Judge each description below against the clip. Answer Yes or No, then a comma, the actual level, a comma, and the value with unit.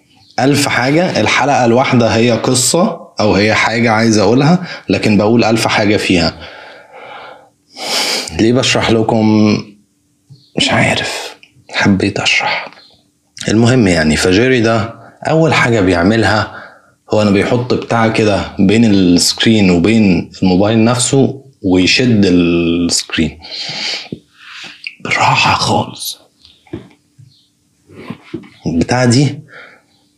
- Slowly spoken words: No, average, 90 wpm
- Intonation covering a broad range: No, average, 4.0 semitones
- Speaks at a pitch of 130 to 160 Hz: No, low, 110 Hz